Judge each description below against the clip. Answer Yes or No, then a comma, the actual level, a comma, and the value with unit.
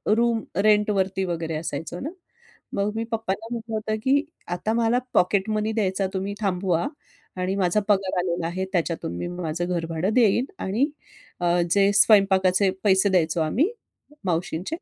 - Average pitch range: Yes, average, 3.4 semitones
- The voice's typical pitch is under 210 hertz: Yes, high, 190 Hz